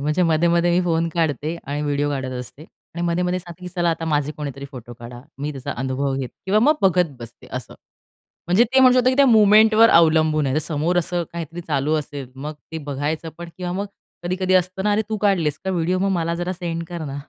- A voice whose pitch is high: No, medium, 165 Hz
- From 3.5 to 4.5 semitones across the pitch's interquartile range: Yes, average, 3.8 semitones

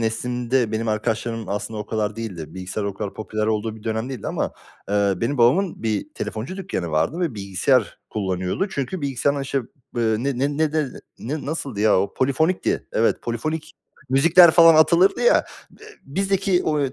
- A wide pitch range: Yes, wide, 6.3 semitones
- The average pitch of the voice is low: Yes, low, 120 Hz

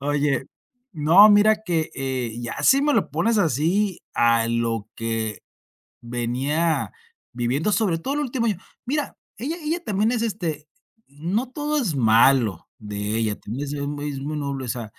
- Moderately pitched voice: Yes, medium, 145 Hz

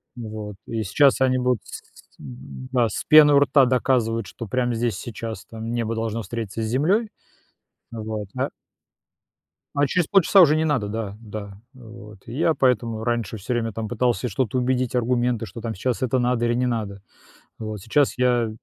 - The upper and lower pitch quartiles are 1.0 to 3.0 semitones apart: Yes, narrow, 2.6 semitones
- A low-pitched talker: Yes, low, 120 Hz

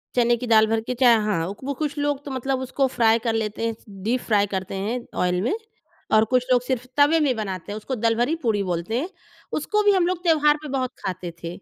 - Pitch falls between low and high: No, high, 240 Hz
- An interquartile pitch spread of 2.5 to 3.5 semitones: No, average, 4.4 semitones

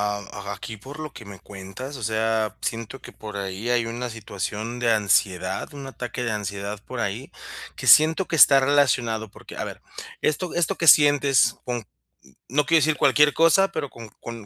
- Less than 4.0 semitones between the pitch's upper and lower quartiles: No, average, 5.1 semitones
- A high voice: No, low, 120 Hz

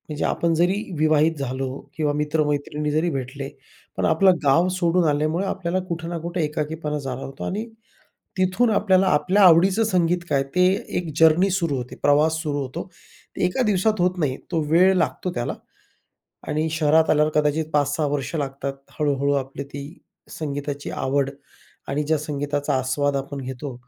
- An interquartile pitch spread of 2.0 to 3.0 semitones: No, average, 3.4 semitones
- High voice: No, medium, 155 Hz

